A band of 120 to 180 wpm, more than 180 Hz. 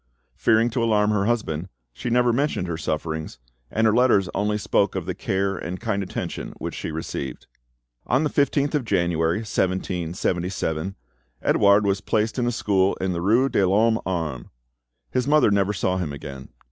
No: average, 170 wpm; low, 100 Hz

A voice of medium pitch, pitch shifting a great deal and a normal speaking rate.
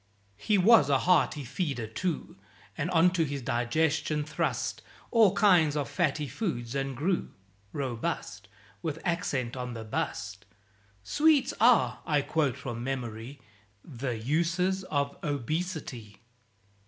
No: medium, 145 Hz; wide, 5.9 semitones; slow, 120 wpm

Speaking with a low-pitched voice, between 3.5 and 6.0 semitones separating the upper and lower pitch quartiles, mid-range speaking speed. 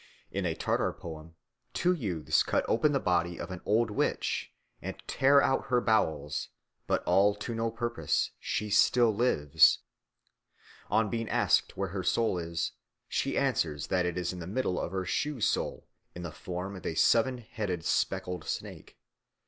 Yes: very low, 95 Hz; average, 4.9 semitones; average, 170 wpm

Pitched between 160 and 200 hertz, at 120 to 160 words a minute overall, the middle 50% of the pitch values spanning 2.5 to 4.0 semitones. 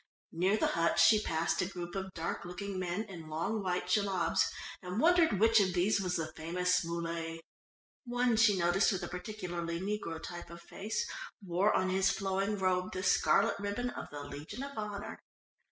No: medium, 185 Hz; average, 180 wpm; average, 3.3 semitones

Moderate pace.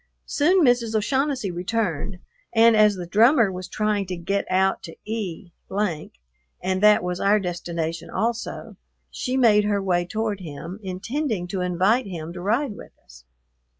Yes: average, 150 wpm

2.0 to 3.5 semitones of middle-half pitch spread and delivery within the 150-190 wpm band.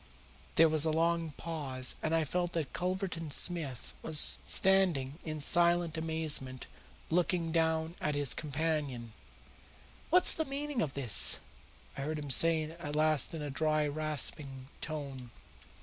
No: narrow, 2.6 semitones; average, 140 wpm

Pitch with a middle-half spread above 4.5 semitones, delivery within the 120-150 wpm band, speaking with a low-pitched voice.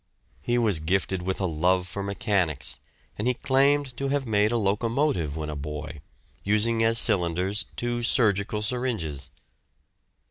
Yes: wide, 5.5 semitones; average, 145 wpm; low, 100 Hz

